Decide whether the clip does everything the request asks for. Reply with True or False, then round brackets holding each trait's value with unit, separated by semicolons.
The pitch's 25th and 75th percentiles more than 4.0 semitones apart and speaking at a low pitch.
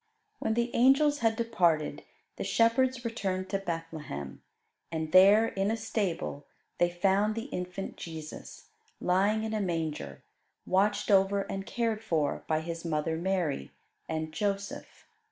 False (5.0 semitones; 195 Hz)